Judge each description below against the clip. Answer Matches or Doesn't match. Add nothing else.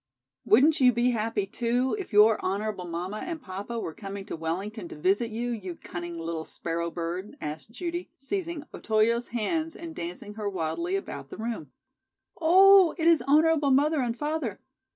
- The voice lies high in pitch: Matches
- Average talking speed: Matches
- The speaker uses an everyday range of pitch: Doesn't match